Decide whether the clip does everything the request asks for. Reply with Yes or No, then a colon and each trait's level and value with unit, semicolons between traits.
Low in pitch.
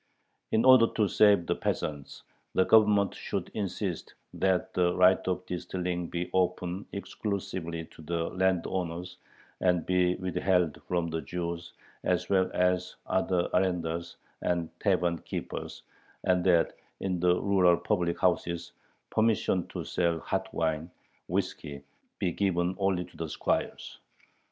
Yes: very low, 90 Hz